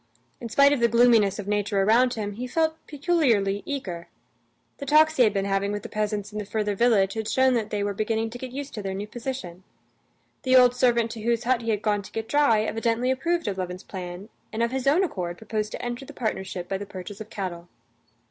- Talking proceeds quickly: Yes, fast, 235 wpm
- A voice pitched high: Yes, high, 220 Hz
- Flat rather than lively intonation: No, average, 3.7 semitones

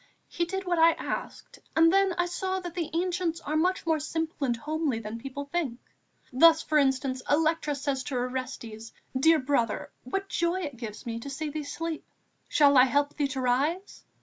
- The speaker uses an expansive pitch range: No, average, 4.3 semitones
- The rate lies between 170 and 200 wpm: Yes, average, 190 wpm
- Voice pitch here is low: No, very high, 295 Hz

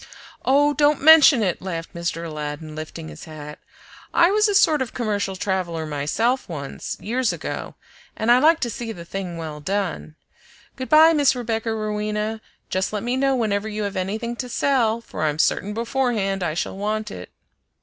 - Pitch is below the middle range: No, high, 210 Hz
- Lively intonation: Yes, wide, 6.7 semitones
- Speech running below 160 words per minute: No, average, 180 wpm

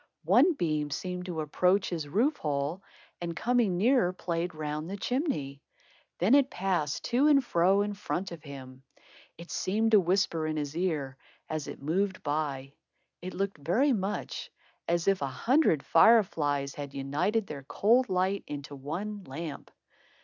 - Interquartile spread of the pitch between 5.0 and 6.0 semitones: Yes, wide, 5.4 semitones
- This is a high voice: No, medium, 175 Hz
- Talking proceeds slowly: No, average, 160 wpm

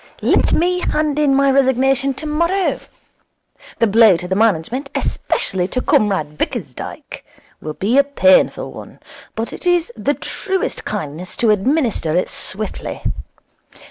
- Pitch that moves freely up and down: Yes, wide, 6.6 semitones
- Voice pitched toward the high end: Yes, very high, 255 Hz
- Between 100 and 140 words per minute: Yes, slow, 135 wpm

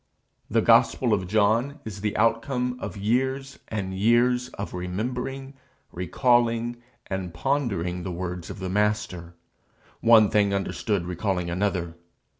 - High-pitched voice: No, low, 105 Hz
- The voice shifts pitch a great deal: No, average, 4.8 semitones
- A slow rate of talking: Yes, slow, 125 wpm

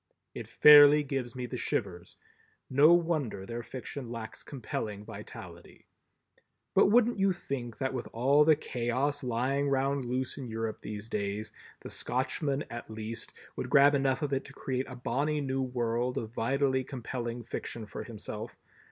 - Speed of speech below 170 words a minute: Yes, average, 160 wpm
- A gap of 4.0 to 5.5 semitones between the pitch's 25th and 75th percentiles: No, average, 3.4 semitones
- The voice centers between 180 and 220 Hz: No, low, 130 Hz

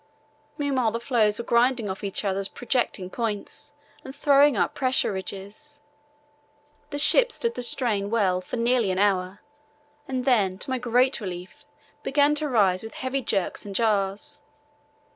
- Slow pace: No, average, 155 wpm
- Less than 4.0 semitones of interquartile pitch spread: No, average, 5.1 semitones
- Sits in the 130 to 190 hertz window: No, high, 230 Hz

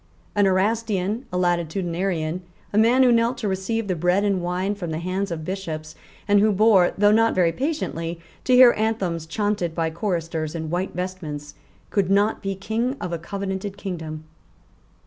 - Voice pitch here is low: No, high, 190 Hz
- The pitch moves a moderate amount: Yes, average, 3.6 semitones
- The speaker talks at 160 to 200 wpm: Yes, average, 170 wpm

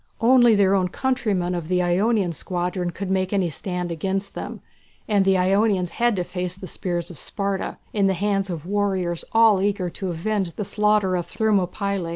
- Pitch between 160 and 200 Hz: Yes, high, 190 Hz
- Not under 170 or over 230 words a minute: Yes, average, 185 wpm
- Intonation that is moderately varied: No, narrow, 2.3 semitones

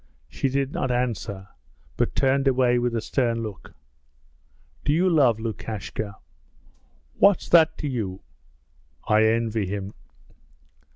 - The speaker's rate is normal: No, slow, 120 wpm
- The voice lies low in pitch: Yes, low, 120 Hz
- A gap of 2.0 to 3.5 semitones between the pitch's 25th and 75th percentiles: No, average, 3.9 semitones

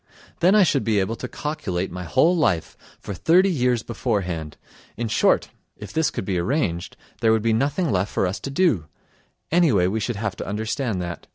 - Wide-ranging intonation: Yes, wide, 7.4 semitones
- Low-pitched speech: Yes, low, 110 Hz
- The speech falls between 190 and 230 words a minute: Yes, average, 195 wpm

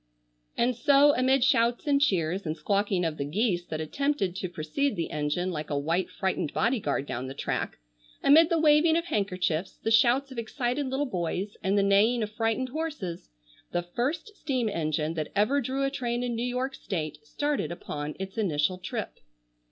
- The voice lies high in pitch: Yes, high, 215 Hz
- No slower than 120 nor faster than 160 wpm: No, average, 185 wpm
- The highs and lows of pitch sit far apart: Yes, wide, 7.5 semitones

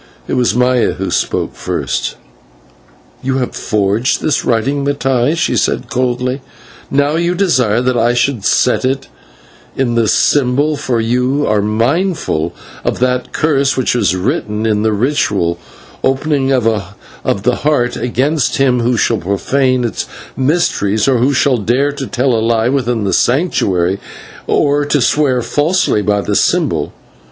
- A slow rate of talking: No, average, 155 wpm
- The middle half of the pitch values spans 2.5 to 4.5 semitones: Yes, average, 3.8 semitones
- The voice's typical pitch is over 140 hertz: No, low, 125 Hz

